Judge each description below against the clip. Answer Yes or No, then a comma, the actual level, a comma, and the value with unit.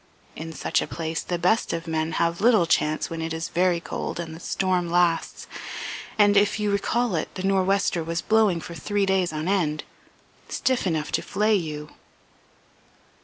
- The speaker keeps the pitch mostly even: No, average, 3.5 semitones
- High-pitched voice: No, medium, 175 Hz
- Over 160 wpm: Yes, average, 175 wpm